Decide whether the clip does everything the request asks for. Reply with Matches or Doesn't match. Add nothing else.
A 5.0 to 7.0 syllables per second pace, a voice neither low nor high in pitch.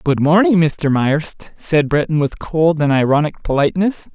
Doesn't match